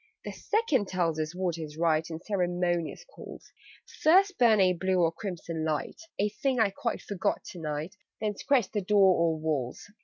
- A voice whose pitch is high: No, medium, 180 Hz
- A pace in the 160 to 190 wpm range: Yes, average, 180 wpm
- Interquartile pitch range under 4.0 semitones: No, average, 4.5 semitones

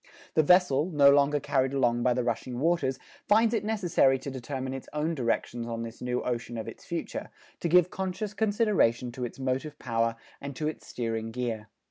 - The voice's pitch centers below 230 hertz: Yes, low, 135 Hz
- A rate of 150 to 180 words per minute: No, average, 190 wpm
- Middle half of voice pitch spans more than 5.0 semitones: Yes, wide, 5.4 semitones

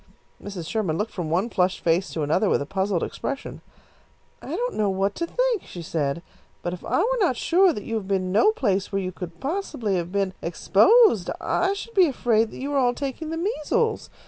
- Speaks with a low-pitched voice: No, high, 210 Hz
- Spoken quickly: Yes, fast, 215 wpm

